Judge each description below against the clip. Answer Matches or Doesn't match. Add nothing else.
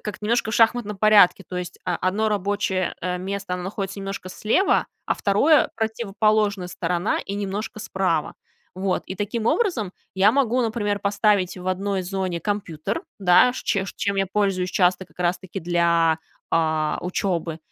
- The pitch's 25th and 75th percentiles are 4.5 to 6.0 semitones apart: Doesn't match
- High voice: Matches